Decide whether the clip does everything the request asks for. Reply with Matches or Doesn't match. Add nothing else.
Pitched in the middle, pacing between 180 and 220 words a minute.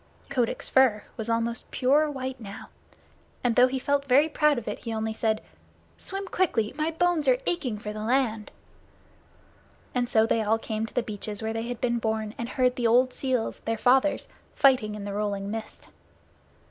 Doesn't match